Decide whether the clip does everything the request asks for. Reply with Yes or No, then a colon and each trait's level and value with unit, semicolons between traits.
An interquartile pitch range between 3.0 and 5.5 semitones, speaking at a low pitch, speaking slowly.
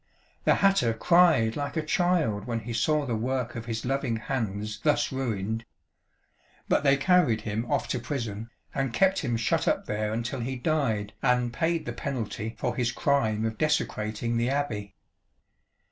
No: average, 4.2 semitones; low, 120 Hz; average, 165 wpm